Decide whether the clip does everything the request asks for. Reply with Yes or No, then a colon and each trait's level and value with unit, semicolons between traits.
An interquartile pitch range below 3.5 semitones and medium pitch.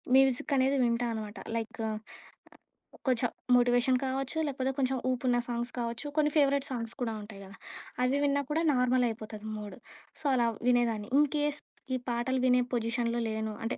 No: narrow, 2.6 semitones; high, 245 Hz